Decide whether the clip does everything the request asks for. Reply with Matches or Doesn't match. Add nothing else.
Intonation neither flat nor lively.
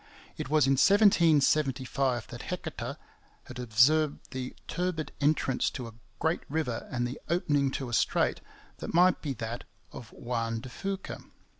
Matches